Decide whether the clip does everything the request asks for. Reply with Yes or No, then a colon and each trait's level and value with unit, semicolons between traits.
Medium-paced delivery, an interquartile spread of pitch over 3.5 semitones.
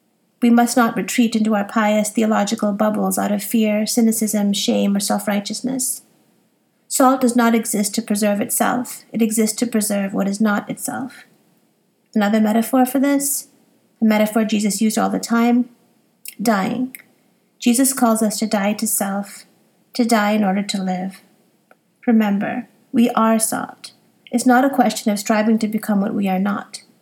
No: average, 160 wpm; narrow, 2.6 semitones